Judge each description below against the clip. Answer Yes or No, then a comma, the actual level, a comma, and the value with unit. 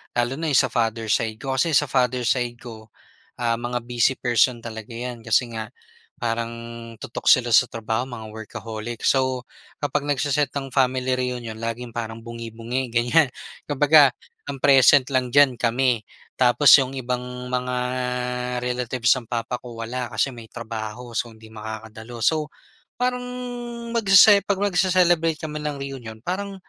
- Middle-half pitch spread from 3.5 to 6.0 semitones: No, average, 2.9 semitones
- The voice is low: Yes, low, 125 Hz